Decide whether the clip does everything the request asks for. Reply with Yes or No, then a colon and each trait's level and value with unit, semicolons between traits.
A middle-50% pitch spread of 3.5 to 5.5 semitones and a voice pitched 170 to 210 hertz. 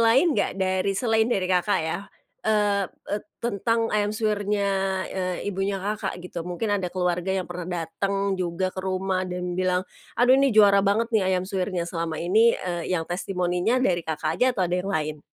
No: narrow, 2.6 semitones; high, 190 Hz